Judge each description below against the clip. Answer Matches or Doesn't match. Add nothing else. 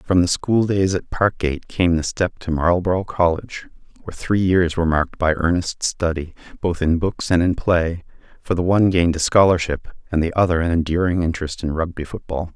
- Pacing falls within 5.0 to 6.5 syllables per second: Matches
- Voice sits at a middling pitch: Doesn't match